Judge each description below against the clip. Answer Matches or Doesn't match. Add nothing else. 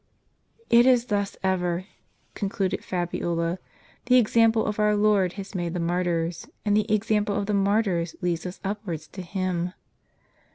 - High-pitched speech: Matches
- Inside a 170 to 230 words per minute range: Doesn't match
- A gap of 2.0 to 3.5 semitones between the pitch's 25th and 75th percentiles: Matches